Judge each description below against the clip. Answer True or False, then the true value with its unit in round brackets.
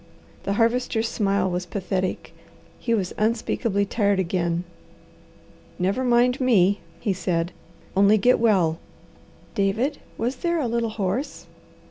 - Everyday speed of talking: False (120 wpm)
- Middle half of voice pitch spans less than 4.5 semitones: True (4.0 semitones)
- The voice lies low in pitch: False (205 Hz)